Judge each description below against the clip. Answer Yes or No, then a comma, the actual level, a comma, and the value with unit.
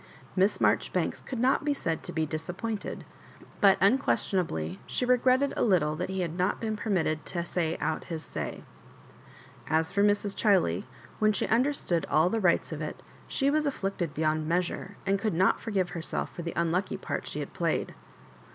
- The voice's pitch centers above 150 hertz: Yes, high, 190 Hz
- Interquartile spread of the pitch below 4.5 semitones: No, average, 4.8 semitones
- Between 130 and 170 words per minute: No, average, 180 wpm